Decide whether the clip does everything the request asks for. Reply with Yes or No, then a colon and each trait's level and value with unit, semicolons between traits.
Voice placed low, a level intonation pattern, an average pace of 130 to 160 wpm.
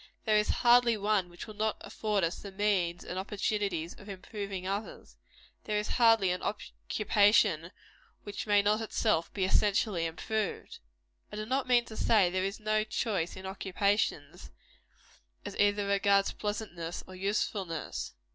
No: high, 205 Hz; narrow, 2.3 semitones; average, 150 wpm